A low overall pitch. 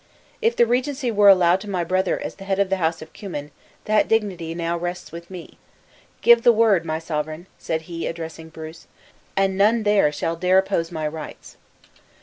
No: medium, 180 Hz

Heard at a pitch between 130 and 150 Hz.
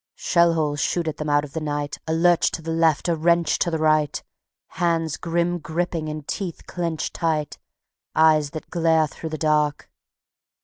No: medium, 160 Hz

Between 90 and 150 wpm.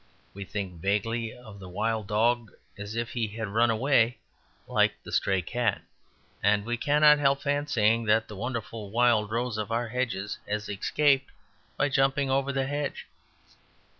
No: average, 160 wpm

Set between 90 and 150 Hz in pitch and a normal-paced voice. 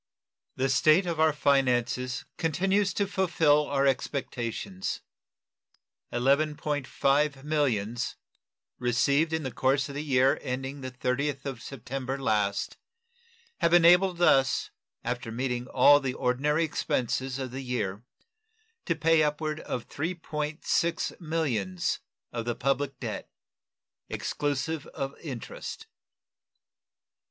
No: medium, 140 Hz; slow, 110 wpm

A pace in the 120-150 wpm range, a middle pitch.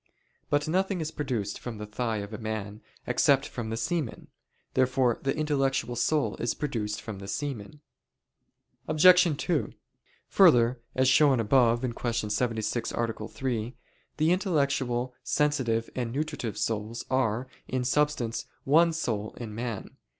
No: slow, 135 wpm; low, 125 Hz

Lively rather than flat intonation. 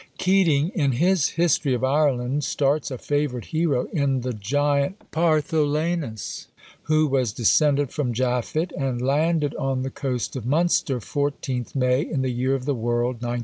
No: average, 3.4 semitones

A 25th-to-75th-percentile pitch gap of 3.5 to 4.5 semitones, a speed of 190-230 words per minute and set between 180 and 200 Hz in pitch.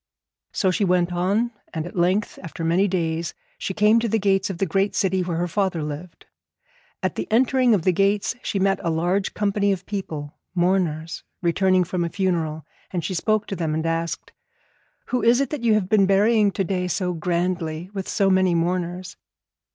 No: average, 2.9 semitones; average, 195 wpm; medium, 185 Hz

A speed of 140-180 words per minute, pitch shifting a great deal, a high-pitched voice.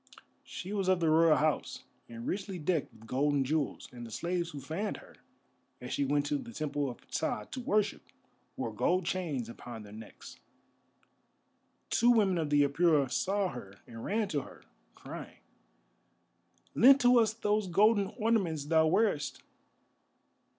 No: average, 160 wpm; wide, 6.4 semitones; medium, 165 Hz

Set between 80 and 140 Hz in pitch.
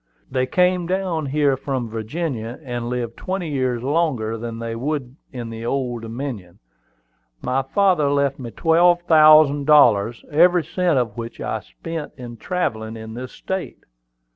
Yes: low, 135 Hz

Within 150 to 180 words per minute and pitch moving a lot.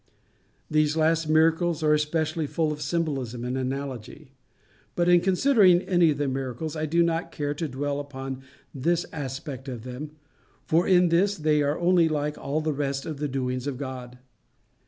No: average, 175 wpm; average, 3.4 semitones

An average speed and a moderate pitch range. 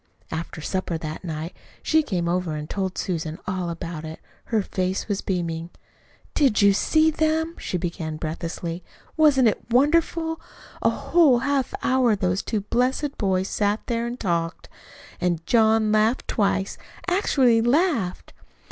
No: average, 145 wpm; wide, 7.0 semitones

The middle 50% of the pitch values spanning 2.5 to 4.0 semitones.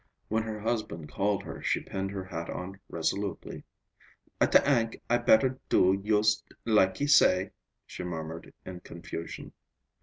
Yes: average, 3.7 semitones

